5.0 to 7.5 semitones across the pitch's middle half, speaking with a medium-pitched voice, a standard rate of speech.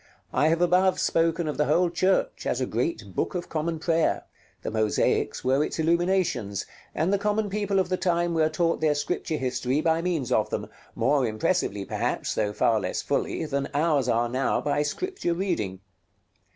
Yes: wide, 5.4 semitones; medium, 160 Hz; average, 180 wpm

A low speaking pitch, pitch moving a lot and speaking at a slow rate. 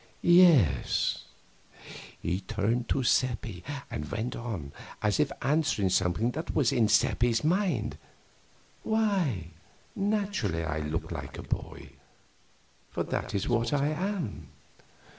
Yes: low, 120 Hz; wide, 9.0 semitones; slow, 120 wpm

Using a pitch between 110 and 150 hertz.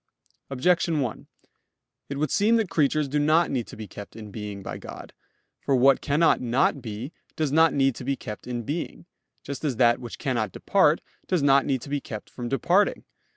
Yes: low, 135 Hz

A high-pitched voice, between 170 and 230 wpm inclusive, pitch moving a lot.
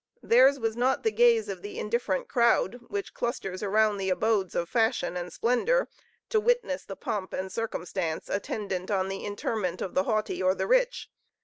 Yes: high, 220 Hz; average, 180 wpm; wide, 6.8 semitones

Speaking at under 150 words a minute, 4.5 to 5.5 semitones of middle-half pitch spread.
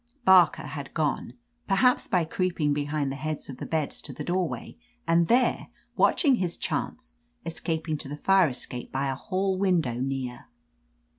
No: average, 165 wpm; average, 5.0 semitones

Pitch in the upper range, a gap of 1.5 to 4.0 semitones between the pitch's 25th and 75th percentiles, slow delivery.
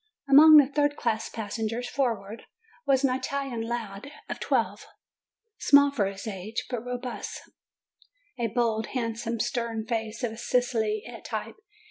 Yes: high, 235 Hz; average, 2.7 semitones; slow, 130 wpm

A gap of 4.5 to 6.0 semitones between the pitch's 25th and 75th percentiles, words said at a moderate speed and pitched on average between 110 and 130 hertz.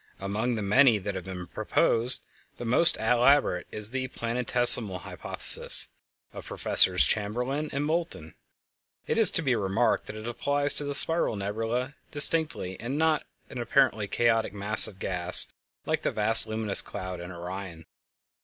Yes: average, 5.2 semitones; average, 155 wpm; low, 115 Hz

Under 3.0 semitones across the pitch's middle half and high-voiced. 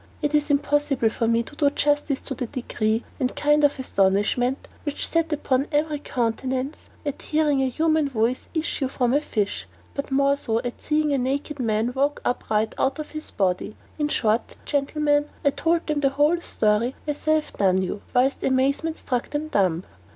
No: average, 3.8 semitones; very high, 275 Hz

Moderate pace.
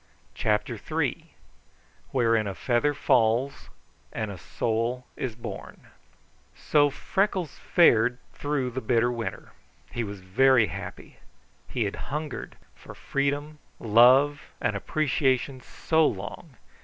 No: slow, 115 wpm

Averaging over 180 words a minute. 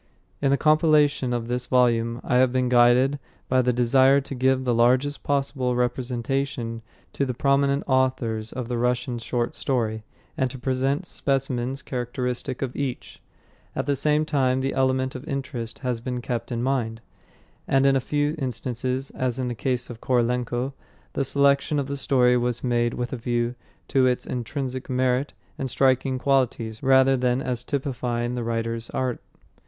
No: average, 170 wpm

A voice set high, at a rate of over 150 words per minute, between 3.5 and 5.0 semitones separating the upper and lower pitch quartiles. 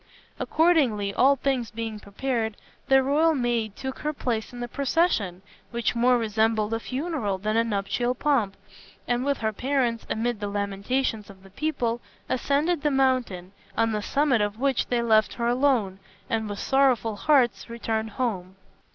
Yes: high, 235 Hz; average, 160 wpm; average, 4.0 semitones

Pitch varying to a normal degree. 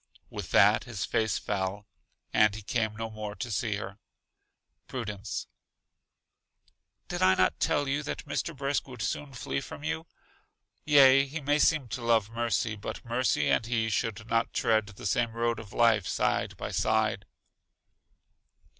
Yes: average, 3.7 semitones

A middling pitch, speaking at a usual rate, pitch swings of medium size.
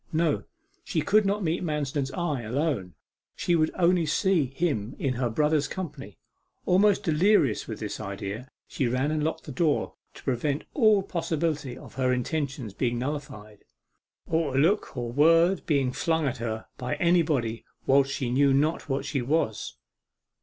Yes: medium, 145 Hz; average, 160 wpm; average, 4.7 semitones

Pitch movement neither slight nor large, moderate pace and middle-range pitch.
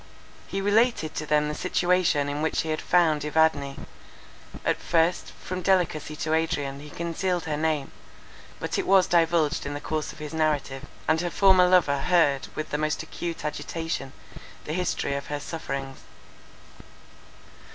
Yes: average, 3.0 semitones; average, 160 wpm; medium, 160 Hz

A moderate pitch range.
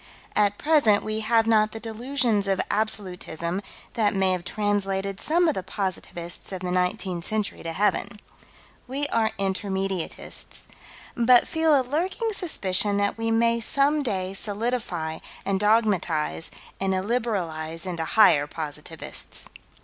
Yes: average, 3.8 semitones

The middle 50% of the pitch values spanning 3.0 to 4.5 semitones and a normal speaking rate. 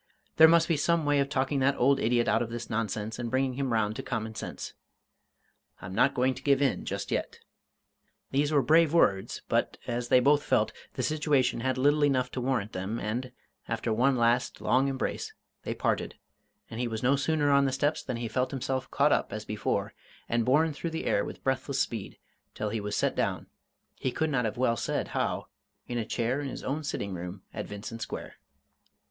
No: average, 3.4 semitones; fast, 210 wpm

